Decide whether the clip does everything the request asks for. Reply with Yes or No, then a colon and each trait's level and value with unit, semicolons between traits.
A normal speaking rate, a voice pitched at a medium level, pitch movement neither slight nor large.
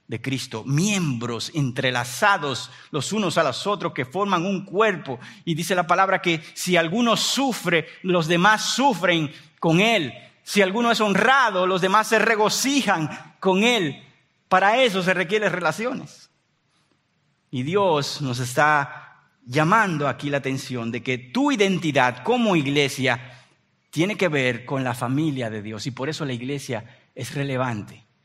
No: average, 150 wpm; medium, 165 Hz; wide, 6.9 semitones